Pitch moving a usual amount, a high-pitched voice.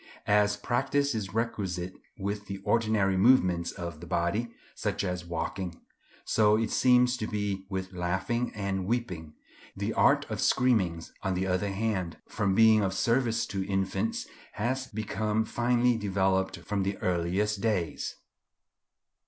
No: average, 3.3 semitones; low, 100 Hz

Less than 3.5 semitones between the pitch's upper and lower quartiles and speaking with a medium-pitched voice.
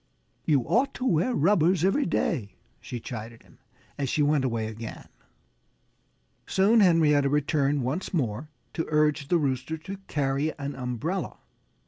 No: average, 4.4 semitones; medium, 150 Hz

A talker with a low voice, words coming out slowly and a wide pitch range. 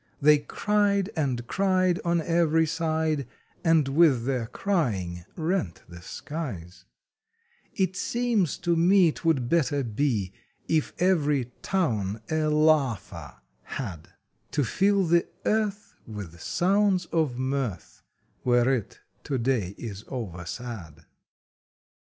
No: medium, 150 Hz; slow, 110 wpm; wide, 6.8 semitones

